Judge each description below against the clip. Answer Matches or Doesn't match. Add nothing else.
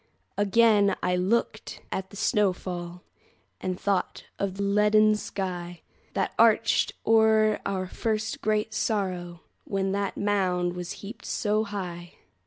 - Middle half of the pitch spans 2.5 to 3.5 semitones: Matches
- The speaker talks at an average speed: Doesn't match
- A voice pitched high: Matches